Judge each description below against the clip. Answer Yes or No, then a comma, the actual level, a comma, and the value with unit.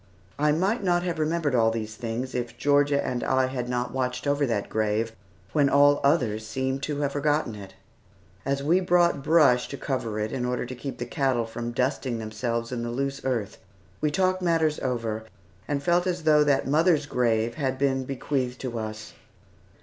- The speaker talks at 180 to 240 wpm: Yes, average, 190 wpm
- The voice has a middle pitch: No, low, 130 Hz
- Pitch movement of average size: Yes, average, 3.8 semitones